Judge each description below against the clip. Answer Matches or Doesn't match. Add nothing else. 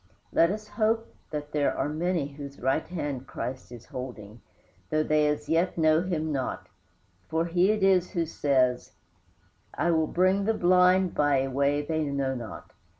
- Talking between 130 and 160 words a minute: Doesn't match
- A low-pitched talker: Doesn't match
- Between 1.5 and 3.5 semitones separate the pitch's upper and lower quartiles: Doesn't match